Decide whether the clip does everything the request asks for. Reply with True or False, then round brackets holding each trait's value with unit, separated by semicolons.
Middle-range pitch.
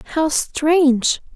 False (295 Hz)